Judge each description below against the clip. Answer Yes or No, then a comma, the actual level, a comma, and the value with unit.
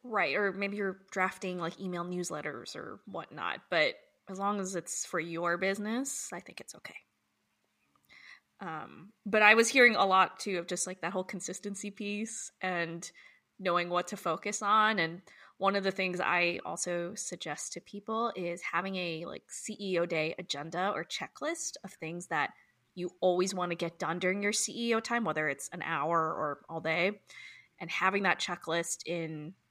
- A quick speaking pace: No, average, 175 wpm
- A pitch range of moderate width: Yes, average, 3.1 semitones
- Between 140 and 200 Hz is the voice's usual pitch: Yes, medium, 185 Hz